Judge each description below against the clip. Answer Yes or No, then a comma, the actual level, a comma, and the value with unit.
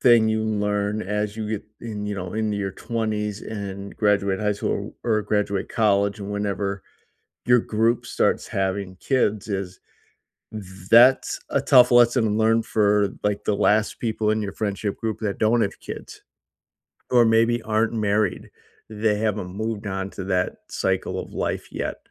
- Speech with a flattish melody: Yes, narrow, 1.7 semitones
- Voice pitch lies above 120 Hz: No, low, 105 Hz